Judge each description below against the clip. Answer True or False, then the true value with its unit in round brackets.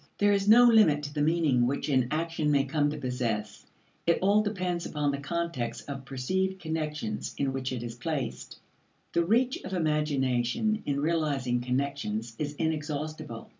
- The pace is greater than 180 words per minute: False (165 wpm)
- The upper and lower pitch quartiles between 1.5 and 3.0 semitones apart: False (4.5 semitones)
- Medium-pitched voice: True (150 Hz)